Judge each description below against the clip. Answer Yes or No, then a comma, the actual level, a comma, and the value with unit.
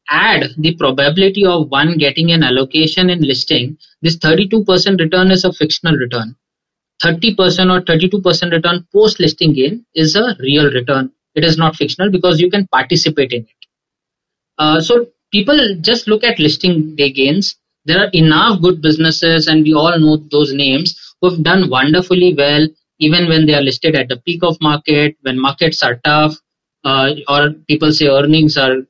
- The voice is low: No, medium, 160 Hz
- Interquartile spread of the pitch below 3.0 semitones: No, average, 3.5 semitones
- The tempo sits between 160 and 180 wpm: Yes, average, 170 wpm